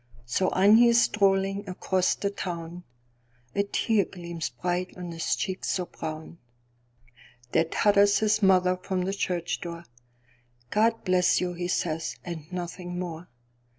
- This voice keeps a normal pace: No, slow, 130 wpm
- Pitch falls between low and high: Yes, medium, 175 Hz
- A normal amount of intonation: No, wide, 7.1 semitones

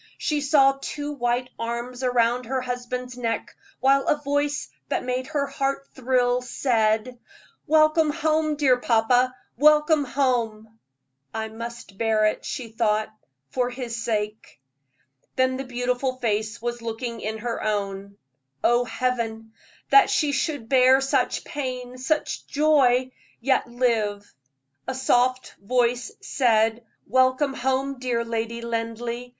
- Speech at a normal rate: No, slow, 130 wpm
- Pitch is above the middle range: Yes, very high, 250 Hz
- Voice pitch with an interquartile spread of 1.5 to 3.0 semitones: Yes, average, 2.7 semitones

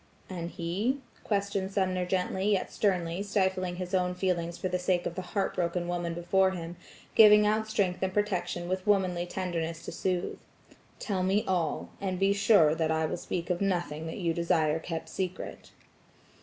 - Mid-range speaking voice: Yes, medium, 180 Hz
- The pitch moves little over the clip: Yes, narrow, 2.1 semitones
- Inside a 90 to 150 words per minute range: No, average, 175 wpm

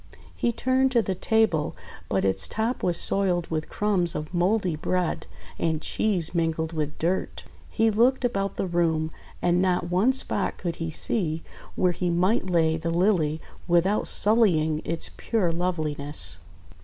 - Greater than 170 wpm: No, average, 155 wpm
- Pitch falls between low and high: Yes, medium, 175 Hz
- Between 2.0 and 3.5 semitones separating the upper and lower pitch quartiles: No, average, 4.1 semitones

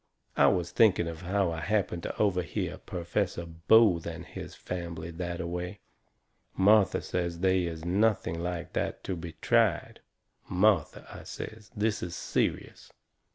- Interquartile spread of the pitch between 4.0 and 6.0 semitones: No, average, 3.0 semitones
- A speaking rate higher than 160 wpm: No, average, 150 wpm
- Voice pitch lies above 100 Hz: No, very low, 90 Hz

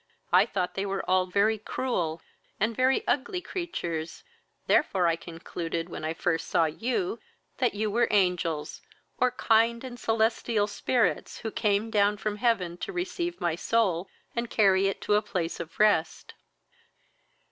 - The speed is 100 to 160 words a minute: Yes, average, 155 wpm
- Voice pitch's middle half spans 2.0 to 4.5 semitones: No, average, 5.0 semitones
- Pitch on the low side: No, high, 205 Hz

